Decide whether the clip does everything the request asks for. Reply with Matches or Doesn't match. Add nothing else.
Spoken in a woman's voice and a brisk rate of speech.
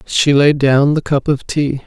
Matches